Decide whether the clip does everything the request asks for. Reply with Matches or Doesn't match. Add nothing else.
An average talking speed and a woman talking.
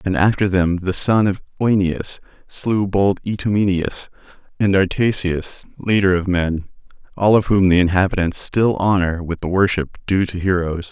Doesn't match